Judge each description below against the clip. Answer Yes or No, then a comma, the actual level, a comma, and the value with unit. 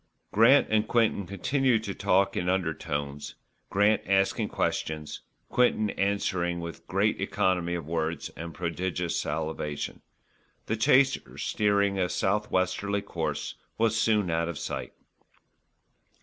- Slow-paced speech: Yes, slow, 120 wpm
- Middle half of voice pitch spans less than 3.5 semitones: No, average, 3.9 semitones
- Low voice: Yes, very low, 95 Hz